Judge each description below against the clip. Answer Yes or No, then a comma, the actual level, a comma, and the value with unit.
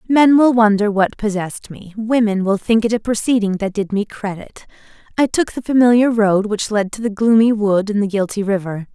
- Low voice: No, high, 215 Hz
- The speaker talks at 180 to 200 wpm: Yes, average, 195 wpm